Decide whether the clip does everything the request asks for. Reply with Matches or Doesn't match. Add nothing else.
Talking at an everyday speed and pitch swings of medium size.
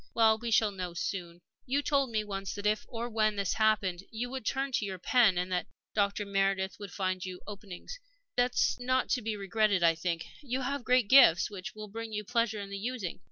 Doesn't match